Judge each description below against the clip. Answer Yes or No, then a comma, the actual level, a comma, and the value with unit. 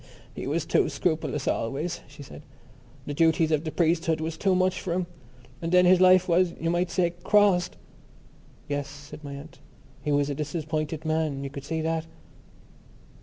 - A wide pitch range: No, average, 3.2 semitones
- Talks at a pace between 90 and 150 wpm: No, average, 175 wpm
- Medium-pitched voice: Yes, medium, 160 Hz